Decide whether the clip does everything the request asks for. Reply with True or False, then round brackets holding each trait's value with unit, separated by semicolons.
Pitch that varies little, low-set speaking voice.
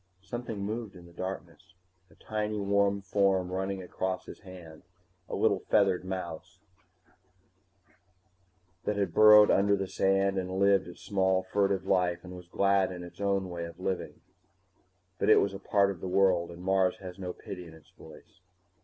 True (1.6 semitones; 95 Hz)